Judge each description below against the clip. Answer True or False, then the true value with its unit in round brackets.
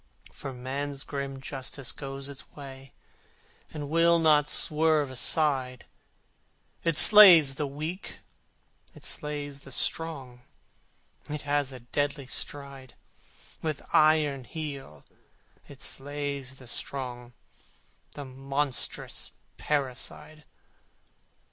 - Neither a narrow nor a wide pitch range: False (2.1 semitones)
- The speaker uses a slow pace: True (100 wpm)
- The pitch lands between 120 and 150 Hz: True (140 Hz)